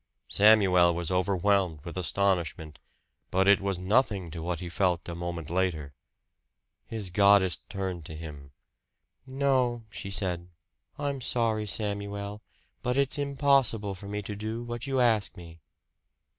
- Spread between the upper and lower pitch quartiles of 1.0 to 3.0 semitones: No, average, 4.1 semitones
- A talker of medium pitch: No, low, 100 Hz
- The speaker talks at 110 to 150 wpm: Yes, average, 140 wpm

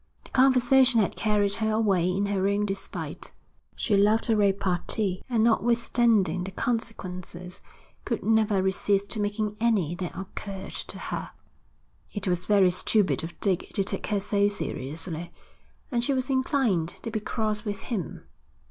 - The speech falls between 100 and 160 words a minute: Yes, average, 150 wpm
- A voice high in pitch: Yes, high, 205 Hz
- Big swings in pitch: No, average, 3.0 semitones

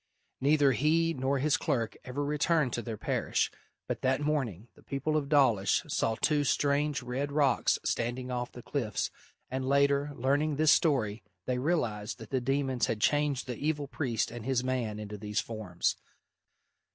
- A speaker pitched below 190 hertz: Yes, low, 135 Hz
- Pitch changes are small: No, average, 3.6 semitones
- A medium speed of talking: Yes, average, 165 wpm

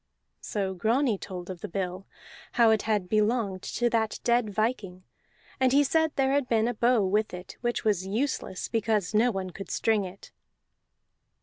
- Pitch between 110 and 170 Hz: No, high, 215 Hz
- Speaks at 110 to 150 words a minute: No, average, 175 wpm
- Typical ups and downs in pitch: Yes, average, 3.9 semitones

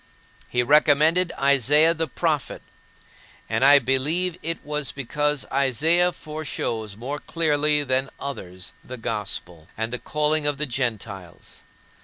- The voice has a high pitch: No, medium, 140 Hz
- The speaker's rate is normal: No, slow, 125 wpm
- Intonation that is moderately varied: Yes, average, 3.9 semitones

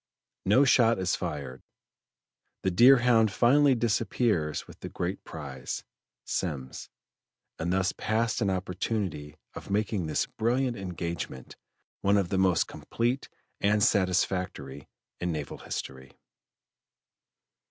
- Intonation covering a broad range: Yes, wide, 5.9 semitones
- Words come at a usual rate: No, slow, 110 wpm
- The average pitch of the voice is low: Yes, very low, 95 Hz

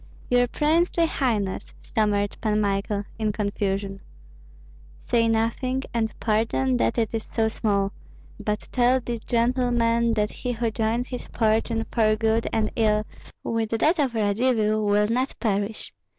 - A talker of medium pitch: No, high, 225 Hz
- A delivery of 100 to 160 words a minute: Yes, average, 140 wpm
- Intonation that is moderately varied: No, narrow, 2.3 semitones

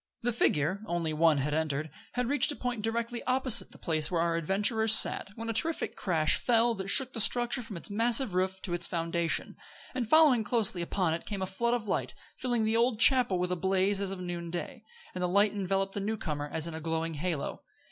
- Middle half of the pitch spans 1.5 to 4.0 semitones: No, wide, 5.5 semitones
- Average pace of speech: No, fast, 220 wpm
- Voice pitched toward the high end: Yes, high, 195 Hz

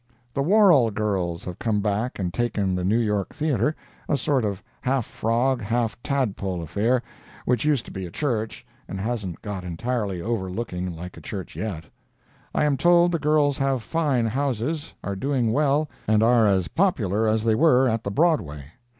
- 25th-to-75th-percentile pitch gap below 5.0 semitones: No, wide, 5.6 semitones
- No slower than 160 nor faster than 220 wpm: Yes, average, 180 wpm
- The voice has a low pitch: Yes, low, 115 Hz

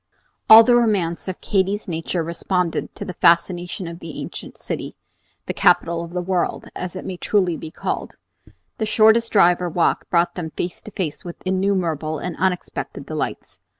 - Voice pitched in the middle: Yes, medium, 180 Hz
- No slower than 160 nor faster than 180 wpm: Yes, average, 175 wpm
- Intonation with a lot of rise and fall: No, narrow, 2.4 semitones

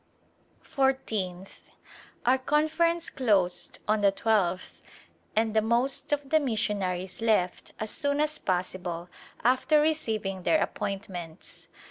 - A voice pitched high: Yes, high, 220 Hz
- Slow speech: Yes, slow, 110 wpm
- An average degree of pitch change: No, wide, 6.6 semitones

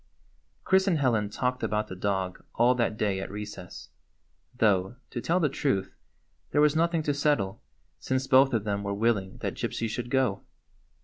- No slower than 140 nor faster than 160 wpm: No, average, 175 wpm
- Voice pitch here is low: Yes, low, 115 Hz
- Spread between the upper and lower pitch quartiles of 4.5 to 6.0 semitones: Yes, average, 5.1 semitones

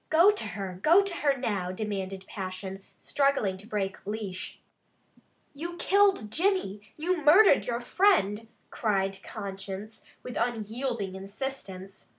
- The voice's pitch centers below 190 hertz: No, high, 215 Hz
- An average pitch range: No, wide, 7.0 semitones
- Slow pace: Yes, slow, 125 wpm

